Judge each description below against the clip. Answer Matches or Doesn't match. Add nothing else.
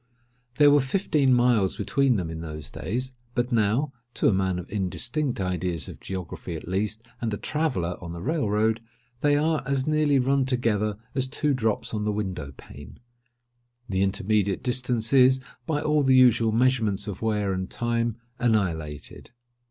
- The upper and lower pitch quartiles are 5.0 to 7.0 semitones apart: Matches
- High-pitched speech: Doesn't match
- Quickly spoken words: Doesn't match